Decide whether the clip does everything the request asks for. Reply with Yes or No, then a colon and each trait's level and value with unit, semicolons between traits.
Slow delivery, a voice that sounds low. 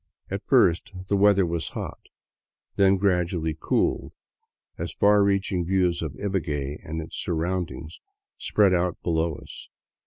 Yes: slow, 130 wpm; very low, 90 Hz